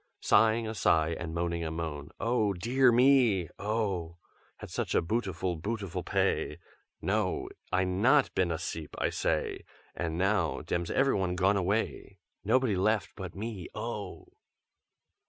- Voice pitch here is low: Yes, very low, 95 Hz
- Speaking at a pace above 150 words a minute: No, slow, 135 wpm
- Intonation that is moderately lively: Yes, average, 4.8 semitones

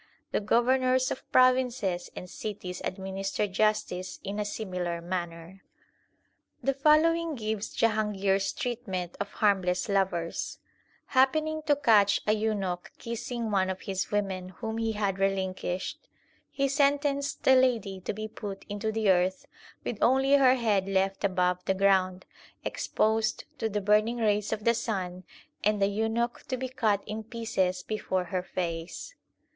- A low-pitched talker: No, high, 210 Hz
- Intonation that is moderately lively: Yes, average, 3.7 semitones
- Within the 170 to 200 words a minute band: No, average, 145 wpm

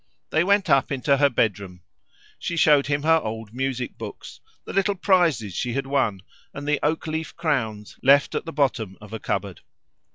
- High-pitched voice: No, medium, 140 Hz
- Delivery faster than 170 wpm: Yes, average, 185 wpm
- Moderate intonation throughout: No, wide, 6.0 semitones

